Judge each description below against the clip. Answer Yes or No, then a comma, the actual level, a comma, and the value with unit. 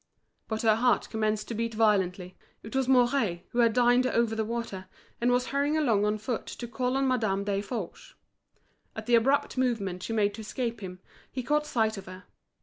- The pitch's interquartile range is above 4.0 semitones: No, average, 3.3 semitones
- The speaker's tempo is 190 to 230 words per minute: Yes, average, 195 wpm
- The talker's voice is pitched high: Yes, high, 225 Hz